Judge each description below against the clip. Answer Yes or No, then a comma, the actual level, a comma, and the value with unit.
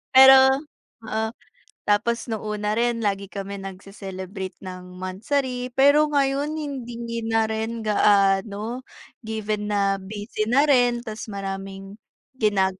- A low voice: No, high, 215 Hz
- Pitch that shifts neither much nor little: Yes, average, 3.6 semitones